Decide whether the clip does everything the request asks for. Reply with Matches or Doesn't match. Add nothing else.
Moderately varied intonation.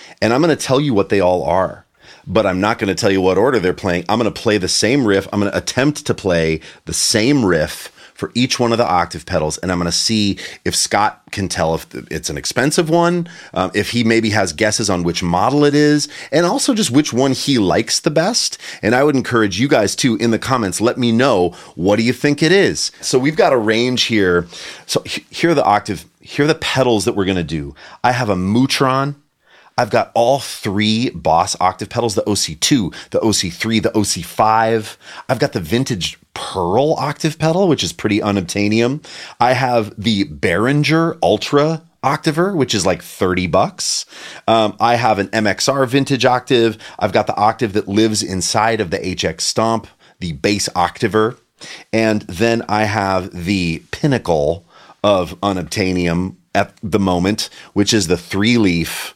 Matches